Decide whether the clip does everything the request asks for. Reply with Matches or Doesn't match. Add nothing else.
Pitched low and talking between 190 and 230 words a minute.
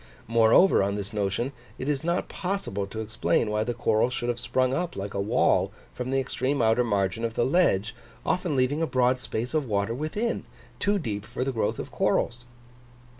Matches